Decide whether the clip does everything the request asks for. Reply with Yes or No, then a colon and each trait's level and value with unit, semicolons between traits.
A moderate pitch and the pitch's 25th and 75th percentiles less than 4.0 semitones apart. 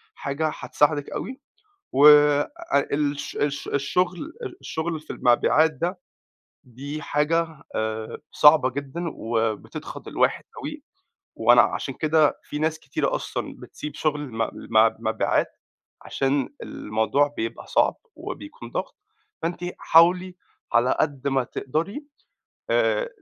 Yes: medium, 150 Hz; average, 3.3 semitones